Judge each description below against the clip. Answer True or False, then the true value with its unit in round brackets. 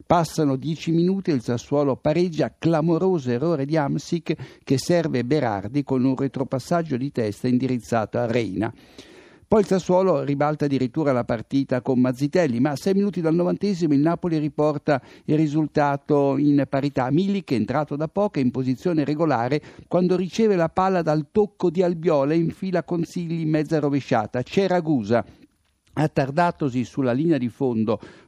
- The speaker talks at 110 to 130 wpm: False (155 wpm)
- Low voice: False (150 Hz)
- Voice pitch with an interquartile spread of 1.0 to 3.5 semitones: False (4.5 semitones)